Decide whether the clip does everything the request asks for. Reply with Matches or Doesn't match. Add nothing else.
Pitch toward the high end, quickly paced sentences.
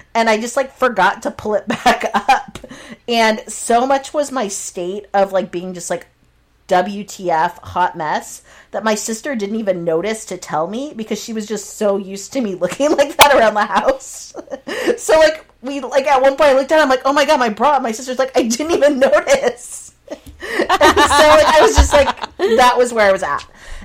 Matches